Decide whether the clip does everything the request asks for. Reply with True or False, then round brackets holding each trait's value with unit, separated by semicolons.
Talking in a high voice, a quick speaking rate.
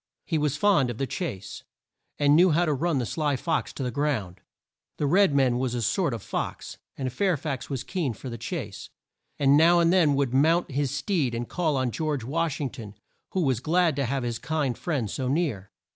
False (140 Hz; 220 wpm)